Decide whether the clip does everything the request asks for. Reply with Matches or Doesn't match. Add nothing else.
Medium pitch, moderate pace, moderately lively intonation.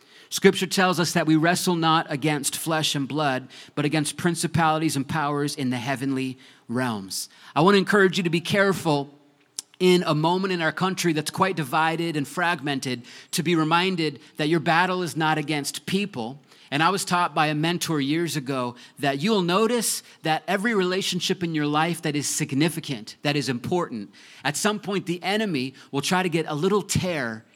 Matches